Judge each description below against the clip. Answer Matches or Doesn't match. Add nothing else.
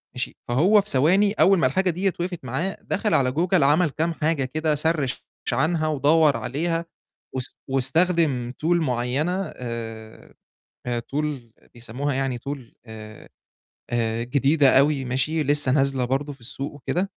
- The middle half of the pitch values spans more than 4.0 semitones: Matches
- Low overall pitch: Doesn't match